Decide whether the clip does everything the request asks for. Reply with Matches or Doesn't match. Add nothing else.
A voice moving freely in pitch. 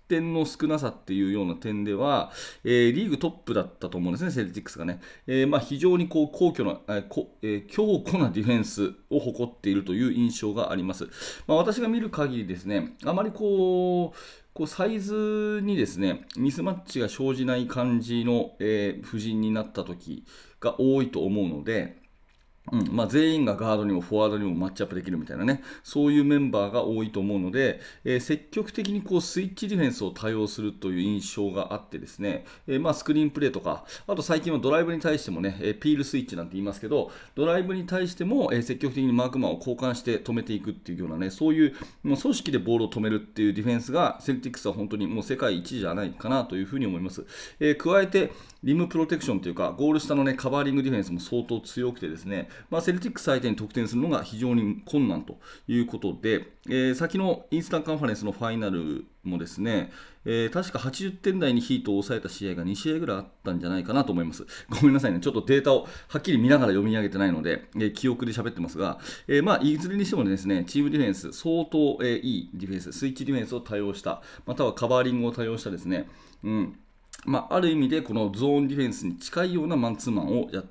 Matches